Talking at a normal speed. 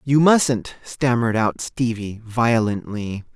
No: slow, 105 wpm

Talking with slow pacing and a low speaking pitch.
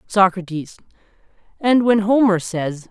No: slow, 105 wpm; high, 195 Hz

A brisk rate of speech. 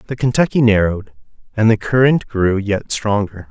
No: average, 155 wpm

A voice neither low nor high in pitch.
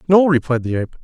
Yes: medium, 150 Hz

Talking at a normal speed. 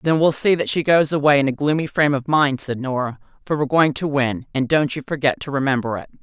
No: fast, 260 wpm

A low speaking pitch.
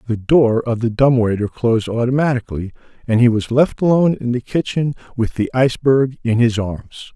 Yes: low, 120 Hz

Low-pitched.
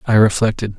Yes: low, 105 Hz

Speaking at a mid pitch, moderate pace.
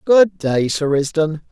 Yes: medium, 160 Hz; average, 160 wpm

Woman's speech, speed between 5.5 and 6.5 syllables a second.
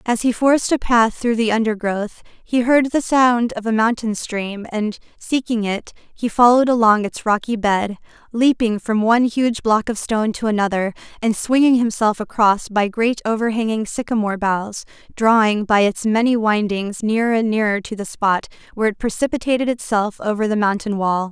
No: female; 5.0 syllables/s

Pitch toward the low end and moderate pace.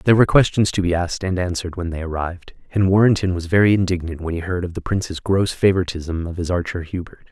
No: very low, 90 Hz; fast, 230 wpm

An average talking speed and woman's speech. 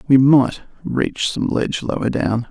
No: average, 165 wpm; male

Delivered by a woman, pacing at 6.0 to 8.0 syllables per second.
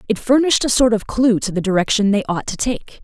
Yes: female; 6.1 syllables/s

